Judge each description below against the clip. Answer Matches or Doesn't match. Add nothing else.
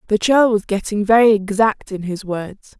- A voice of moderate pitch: Doesn't match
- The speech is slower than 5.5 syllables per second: Matches